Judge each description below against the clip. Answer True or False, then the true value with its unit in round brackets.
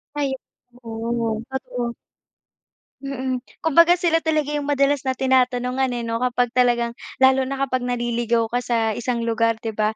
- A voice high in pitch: True (250 Hz)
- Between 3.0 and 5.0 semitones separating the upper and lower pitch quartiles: False (2.4 semitones)